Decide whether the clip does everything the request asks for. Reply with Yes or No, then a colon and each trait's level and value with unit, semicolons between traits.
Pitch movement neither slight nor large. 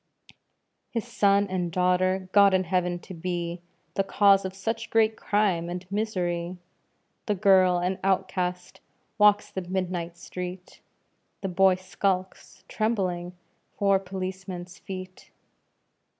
No: narrow, 1.6 semitones